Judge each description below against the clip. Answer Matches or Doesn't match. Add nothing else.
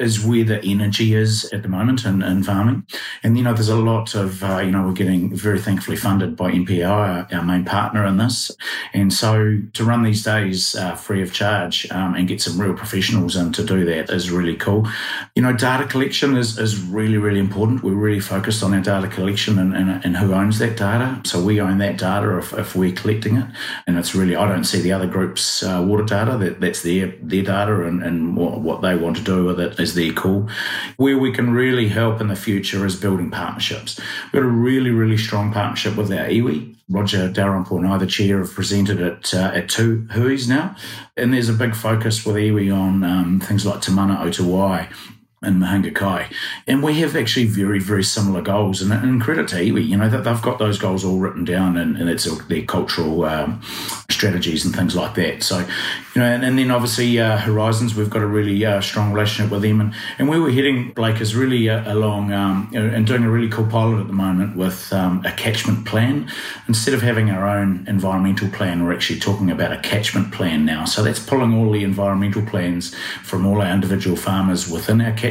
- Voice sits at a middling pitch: Doesn't match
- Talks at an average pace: Doesn't match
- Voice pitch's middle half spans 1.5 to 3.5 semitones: Matches